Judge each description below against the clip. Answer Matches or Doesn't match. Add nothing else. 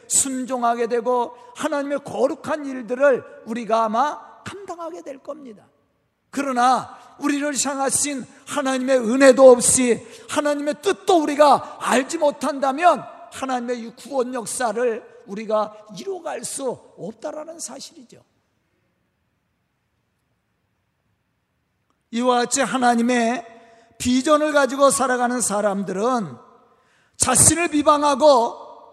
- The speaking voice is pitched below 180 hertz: Doesn't match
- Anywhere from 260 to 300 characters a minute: Doesn't match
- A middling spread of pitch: Matches